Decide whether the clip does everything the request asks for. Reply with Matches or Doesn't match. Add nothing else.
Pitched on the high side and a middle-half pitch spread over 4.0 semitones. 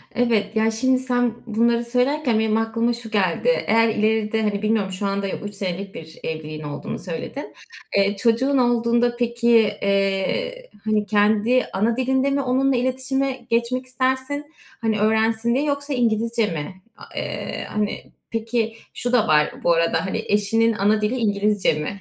Doesn't match